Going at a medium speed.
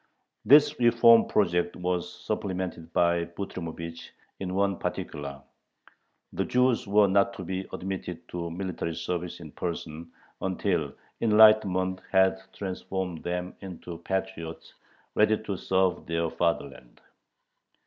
No: slow, 115 wpm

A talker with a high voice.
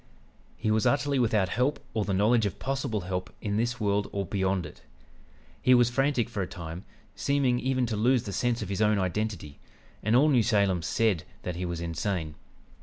No: low, 105 Hz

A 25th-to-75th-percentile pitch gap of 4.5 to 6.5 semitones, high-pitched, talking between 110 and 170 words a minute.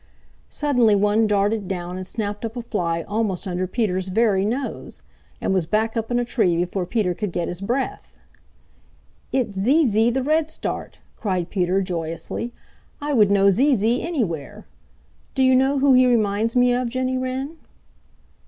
Yes: average, 4.9 semitones; high, 220 Hz; average, 165 wpm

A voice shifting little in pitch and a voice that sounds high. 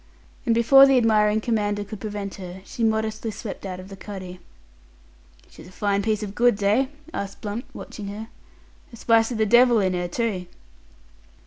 Yes: narrow, 2.3 semitones; high, 210 Hz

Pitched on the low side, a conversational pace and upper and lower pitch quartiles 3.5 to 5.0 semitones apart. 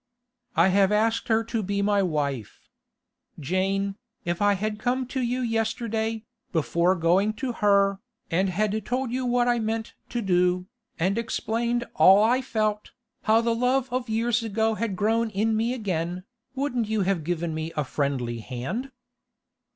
No: high, 215 Hz; average, 160 wpm; average, 3.9 semitones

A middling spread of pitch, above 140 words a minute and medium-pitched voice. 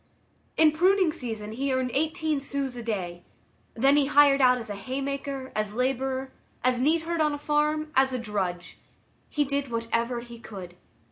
No: average, 4.0 semitones; average, 180 wpm; very high, 265 Hz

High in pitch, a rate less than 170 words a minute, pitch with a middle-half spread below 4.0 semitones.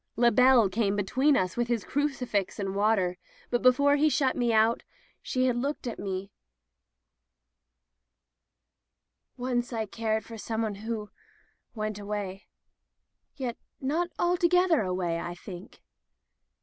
No: high, 225 Hz; slow, 135 wpm; average, 4.7 semitones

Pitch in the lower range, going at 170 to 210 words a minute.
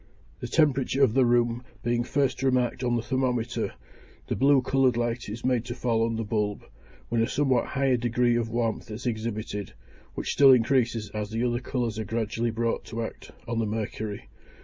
Yes: low, 120 Hz; average, 190 wpm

